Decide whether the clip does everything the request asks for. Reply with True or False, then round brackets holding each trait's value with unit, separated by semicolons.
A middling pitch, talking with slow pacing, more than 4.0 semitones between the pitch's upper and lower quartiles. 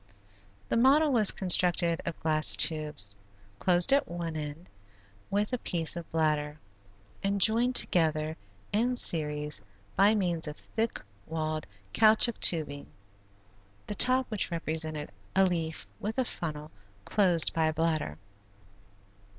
True (170 Hz; 125 wpm; 5.0 semitones)